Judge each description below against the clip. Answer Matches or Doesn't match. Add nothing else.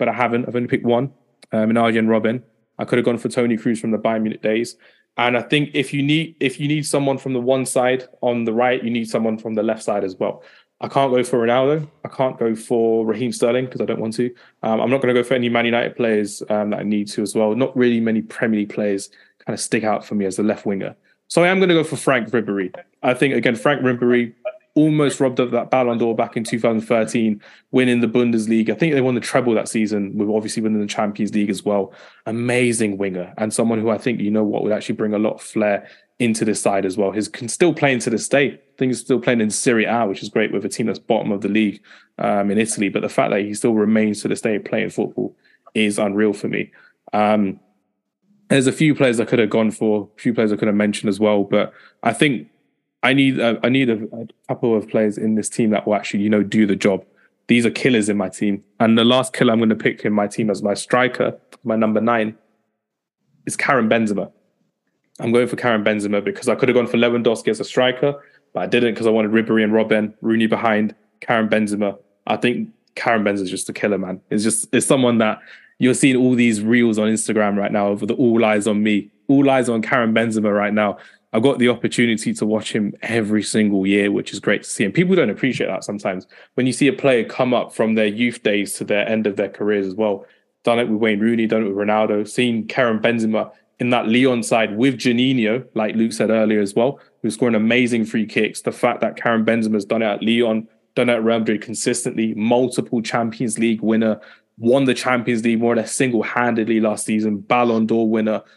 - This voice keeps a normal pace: Doesn't match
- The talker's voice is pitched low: Matches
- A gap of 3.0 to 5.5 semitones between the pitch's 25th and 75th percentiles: Doesn't match